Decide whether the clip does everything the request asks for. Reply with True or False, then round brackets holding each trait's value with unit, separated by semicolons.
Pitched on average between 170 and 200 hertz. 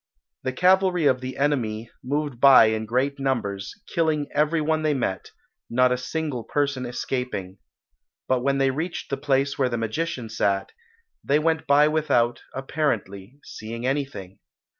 False (135 Hz)